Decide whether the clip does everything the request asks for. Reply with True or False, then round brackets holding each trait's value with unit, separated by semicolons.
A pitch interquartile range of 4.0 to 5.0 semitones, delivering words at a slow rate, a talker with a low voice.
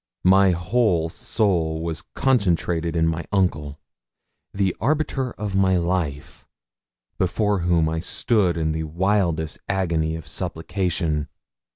False (3.4 semitones; 115 wpm; 85 Hz)